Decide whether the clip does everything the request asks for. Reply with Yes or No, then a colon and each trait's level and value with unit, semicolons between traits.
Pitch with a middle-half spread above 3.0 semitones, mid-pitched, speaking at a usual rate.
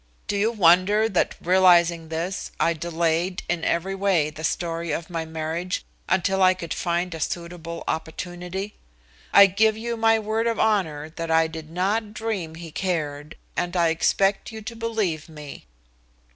Yes: average, 3.4 semitones; medium, 175 Hz; average, 160 wpm